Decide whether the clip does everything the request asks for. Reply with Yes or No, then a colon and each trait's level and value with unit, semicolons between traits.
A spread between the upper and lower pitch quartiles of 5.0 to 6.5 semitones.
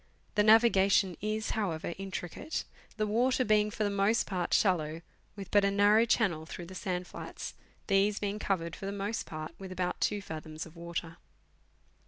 No: average, 3.4 semitones